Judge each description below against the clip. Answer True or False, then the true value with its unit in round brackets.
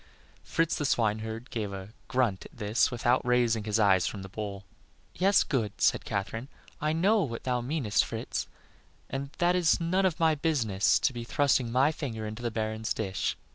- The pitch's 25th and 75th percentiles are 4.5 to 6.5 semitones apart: True (5.4 semitones)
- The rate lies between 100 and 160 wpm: False (185 wpm)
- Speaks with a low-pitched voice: True (120 Hz)